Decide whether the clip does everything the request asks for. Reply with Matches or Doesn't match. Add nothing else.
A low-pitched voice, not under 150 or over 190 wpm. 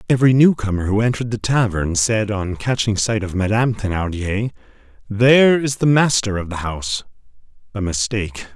Matches